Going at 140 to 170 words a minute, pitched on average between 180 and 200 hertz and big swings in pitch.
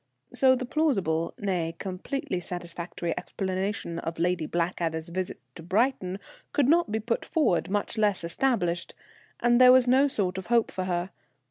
Yes: average, 155 wpm; high, 190 Hz; wide, 5.7 semitones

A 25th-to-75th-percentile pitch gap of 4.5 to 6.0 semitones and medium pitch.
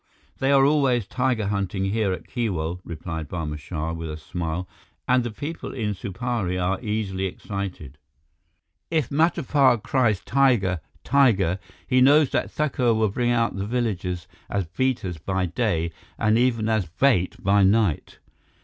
No: wide, 5.6 semitones; low, 105 Hz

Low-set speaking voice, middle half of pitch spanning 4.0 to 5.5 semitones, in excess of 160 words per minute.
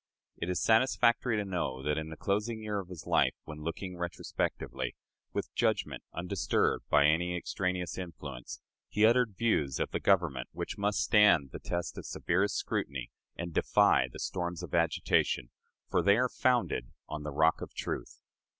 Yes: very low, 90 Hz; average, 4.8 semitones; average, 170 wpm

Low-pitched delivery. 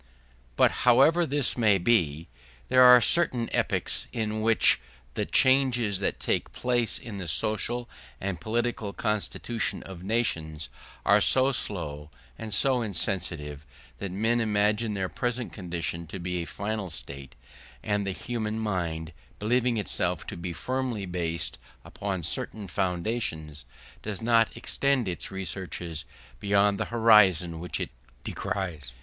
Yes: low, 100 Hz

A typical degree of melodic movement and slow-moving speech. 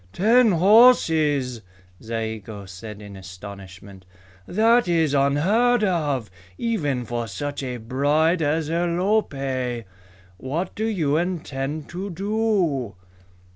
No: wide, 7.6 semitones; slow, 100 wpm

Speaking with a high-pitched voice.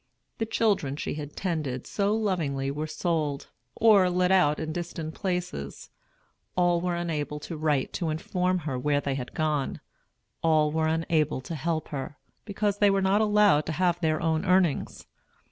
No: medium, 160 Hz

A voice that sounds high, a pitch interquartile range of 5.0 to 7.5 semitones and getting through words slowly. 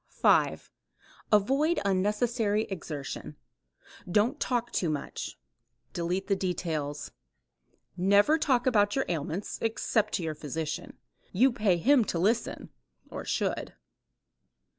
Yes: high, 205 Hz; wide, 5.5 semitones; slow, 110 wpm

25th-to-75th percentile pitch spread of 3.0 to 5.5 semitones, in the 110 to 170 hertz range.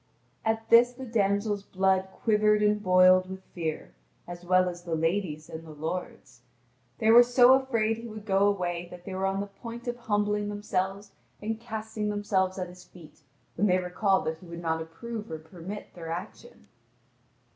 No: average, 3.3 semitones; high, 195 Hz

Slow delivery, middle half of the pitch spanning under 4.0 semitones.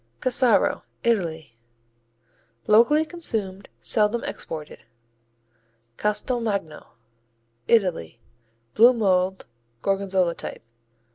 No: slow, 65 wpm; average, 4.3 semitones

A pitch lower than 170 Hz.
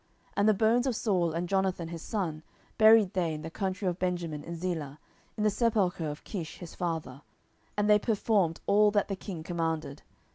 No: medium, 180 Hz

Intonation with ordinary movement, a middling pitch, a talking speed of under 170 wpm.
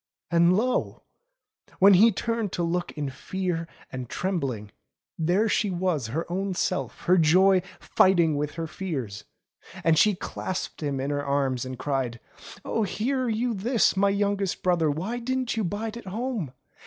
No: wide, 5.8 semitones; medium, 180 Hz; average, 160 wpm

